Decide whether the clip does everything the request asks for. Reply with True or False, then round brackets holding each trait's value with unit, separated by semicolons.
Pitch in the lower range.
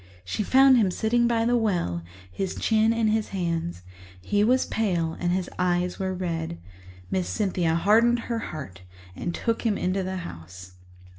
False (190 Hz)